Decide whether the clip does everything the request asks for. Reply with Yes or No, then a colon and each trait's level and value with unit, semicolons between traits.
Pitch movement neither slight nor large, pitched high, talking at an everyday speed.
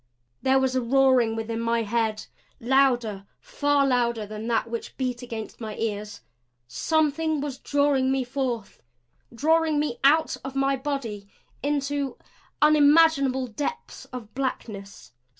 No: average, 3.9 semitones; very high, 260 Hz; slow, 130 wpm